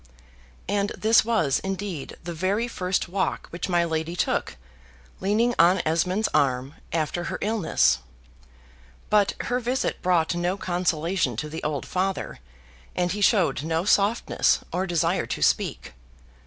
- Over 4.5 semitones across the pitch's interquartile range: No, average, 3.7 semitones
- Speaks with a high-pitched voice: No, medium, 180 Hz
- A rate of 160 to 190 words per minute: No, average, 140 wpm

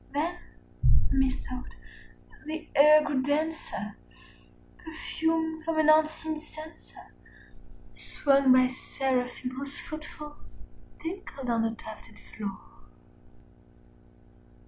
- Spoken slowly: Yes, slow, 90 wpm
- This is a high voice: Yes, very high, 300 Hz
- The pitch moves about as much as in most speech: Yes, average, 3.5 semitones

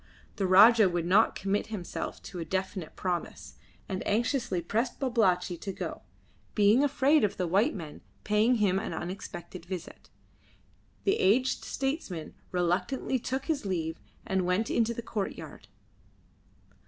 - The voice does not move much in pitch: No, average, 4.5 semitones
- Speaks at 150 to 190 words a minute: No, average, 140 wpm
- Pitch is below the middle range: No, high, 200 Hz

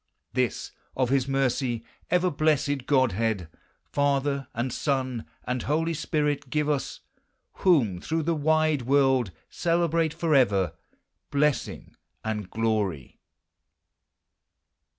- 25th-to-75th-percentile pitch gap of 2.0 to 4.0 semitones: No, average, 4.4 semitones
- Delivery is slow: Yes, slow, 110 wpm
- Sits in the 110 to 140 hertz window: Yes, low, 135 Hz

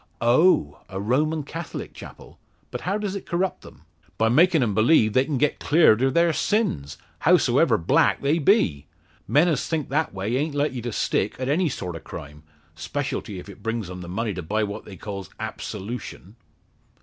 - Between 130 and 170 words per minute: No, average, 185 wpm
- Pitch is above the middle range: No, low, 130 Hz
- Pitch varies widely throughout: Yes, wide, 8.0 semitones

